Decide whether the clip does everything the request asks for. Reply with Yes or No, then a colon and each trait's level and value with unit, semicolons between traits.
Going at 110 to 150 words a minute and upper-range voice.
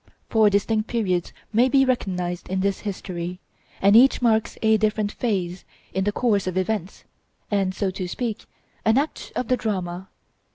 No: average, 165 wpm; high, 205 Hz